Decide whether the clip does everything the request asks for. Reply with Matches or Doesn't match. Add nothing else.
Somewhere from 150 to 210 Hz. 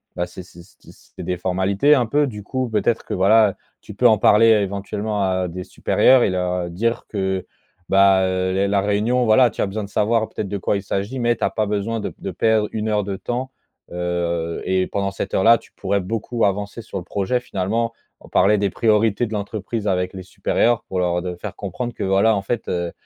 Doesn't match